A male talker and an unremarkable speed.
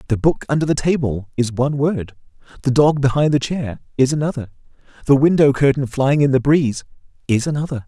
Yes: male; average, 185 wpm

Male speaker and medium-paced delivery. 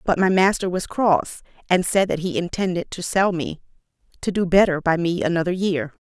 No: female; average, 190 wpm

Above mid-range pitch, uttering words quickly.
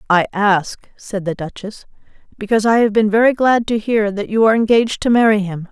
Yes: high, 210 Hz; fast, 210 wpm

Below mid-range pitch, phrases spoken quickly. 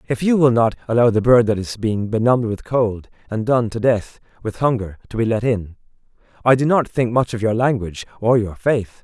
Yes: low, 115 Hz; fast, 225 wpm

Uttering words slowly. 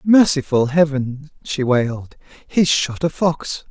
Yes: slow, 130 wpm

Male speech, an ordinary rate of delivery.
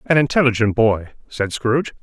Yes: male; average, 150 wpm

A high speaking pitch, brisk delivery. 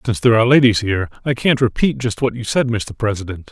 No: low, 115 Hz; fast, 240 wpm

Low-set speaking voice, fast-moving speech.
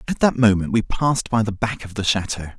Yes: low, 110 Hz; fast, 255 wpm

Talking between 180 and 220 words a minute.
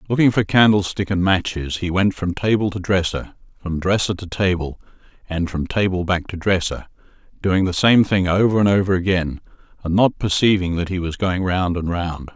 Yes: average, 190 wpm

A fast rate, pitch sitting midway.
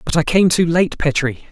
Yes: fast, 240 wpm; medium, 160 Hz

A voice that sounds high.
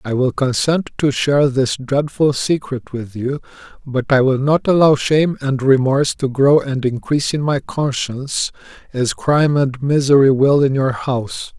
No: low, 135 Hz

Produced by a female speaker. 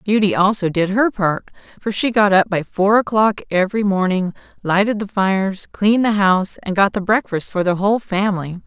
Yes: female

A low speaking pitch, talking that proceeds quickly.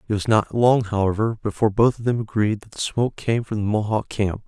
Yes: low, 110 Hz; fast, 240 wpm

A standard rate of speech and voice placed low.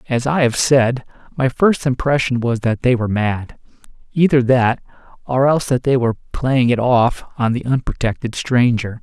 Yes: average, 175 wpm; low, 125 Hz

